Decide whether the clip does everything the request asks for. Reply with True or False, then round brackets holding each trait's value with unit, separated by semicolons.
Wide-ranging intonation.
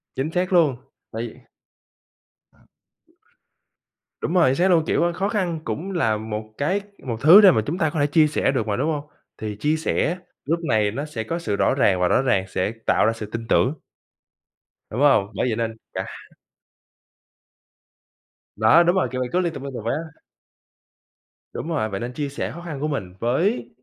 True (6.7 semitones)